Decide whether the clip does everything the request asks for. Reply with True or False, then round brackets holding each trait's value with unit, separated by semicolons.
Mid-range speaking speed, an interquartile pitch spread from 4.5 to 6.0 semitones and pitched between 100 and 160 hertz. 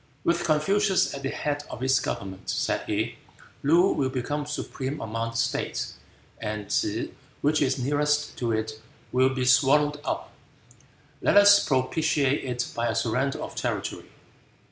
False (150 wpm; 3.3 semitones; 135 Hz)